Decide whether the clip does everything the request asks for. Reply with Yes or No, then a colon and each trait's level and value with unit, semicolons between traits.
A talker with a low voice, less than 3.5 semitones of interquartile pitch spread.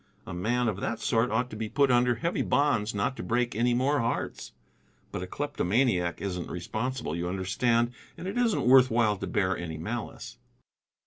No: low, 115 Hz; average, 4.3 semitones